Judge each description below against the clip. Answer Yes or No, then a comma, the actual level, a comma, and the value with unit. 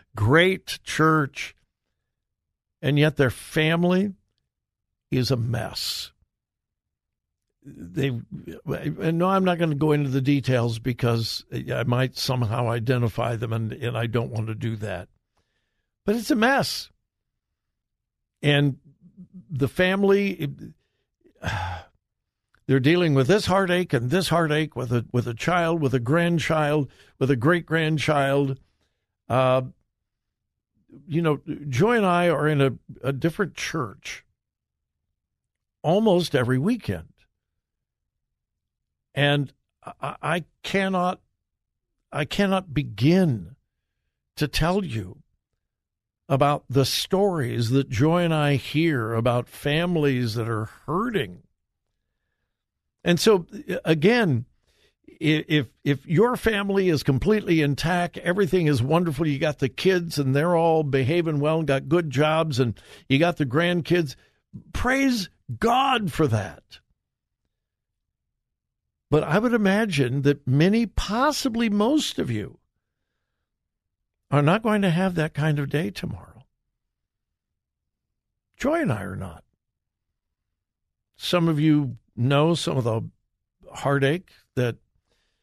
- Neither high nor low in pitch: Yes, medium, 150 Hz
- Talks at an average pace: No, slow, 120 wpm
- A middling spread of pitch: No, wide, 5.8 semitones